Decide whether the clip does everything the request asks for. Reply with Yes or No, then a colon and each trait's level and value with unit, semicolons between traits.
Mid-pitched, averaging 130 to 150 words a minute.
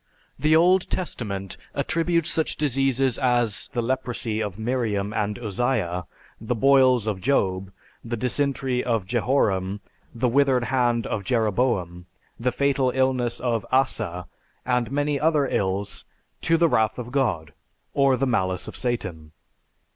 No: low, 120 Hz; slow, 135 wpm